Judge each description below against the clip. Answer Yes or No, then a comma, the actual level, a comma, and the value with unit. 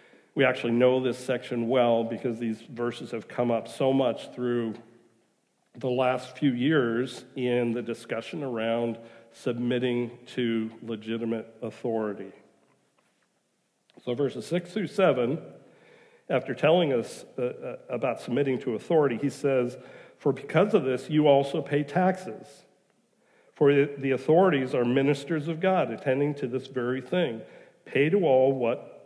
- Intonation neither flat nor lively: Yes, average, 3.2 semitones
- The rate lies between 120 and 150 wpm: Yes, slow, 135 wpm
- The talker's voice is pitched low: Yes, low, 125 Hz